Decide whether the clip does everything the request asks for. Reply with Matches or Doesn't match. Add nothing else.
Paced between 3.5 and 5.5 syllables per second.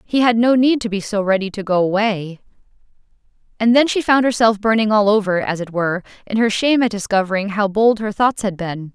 Doesn't match